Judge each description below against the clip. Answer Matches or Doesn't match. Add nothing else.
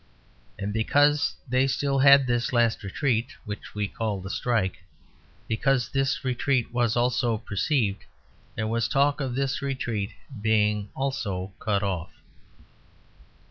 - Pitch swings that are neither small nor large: Matches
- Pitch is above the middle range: Doesn't match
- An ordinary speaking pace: Doesn't match